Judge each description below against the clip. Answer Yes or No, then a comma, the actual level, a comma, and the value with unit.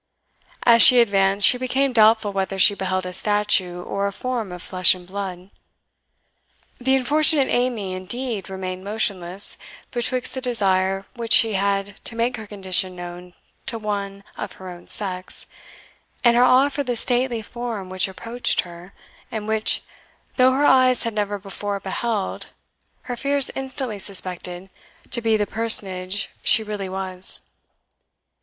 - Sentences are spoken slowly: No, average, 150 wpm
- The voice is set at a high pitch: Yes, high, 205 Hz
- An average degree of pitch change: Yes, average, 4.2 semitones